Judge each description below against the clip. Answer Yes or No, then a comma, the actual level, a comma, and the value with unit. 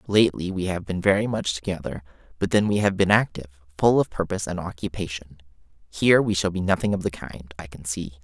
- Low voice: Yes, very low, 90 Hz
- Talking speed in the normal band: No, fast, 210 wpm